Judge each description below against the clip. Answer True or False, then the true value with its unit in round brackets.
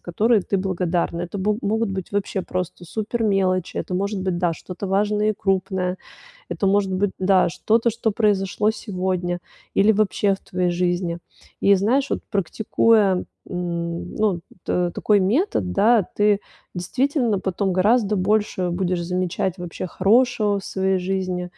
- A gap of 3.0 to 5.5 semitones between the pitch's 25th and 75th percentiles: False (2.6 semitones)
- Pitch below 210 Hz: True (190 Hz)